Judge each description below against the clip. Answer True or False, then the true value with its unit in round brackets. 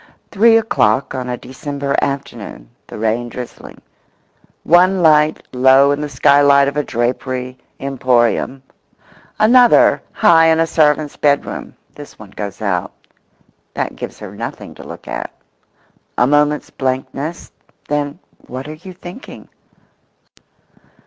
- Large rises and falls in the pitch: False (3.4 semitones)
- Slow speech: True (120 wpm)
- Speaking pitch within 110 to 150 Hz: True (140 Hz)